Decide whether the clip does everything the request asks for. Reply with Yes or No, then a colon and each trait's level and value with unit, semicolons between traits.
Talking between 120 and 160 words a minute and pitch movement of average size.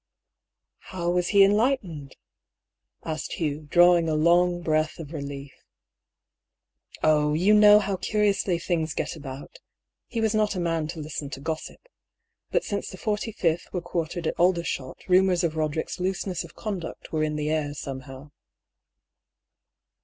Yes: average, 155 wpm; average, 3.6 semitones